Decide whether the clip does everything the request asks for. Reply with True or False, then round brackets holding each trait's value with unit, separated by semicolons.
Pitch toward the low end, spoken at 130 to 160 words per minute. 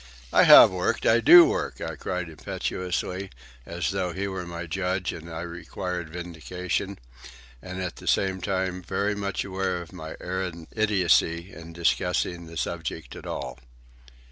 True (90 Hz; 155 wpm)